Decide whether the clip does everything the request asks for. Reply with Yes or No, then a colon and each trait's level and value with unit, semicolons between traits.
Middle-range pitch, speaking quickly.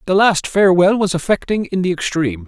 No: medium, 180 Hz; average, 195 wpm